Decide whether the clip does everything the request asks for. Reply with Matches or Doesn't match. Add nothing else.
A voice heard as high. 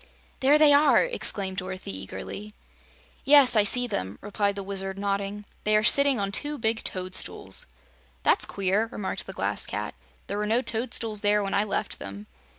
Matches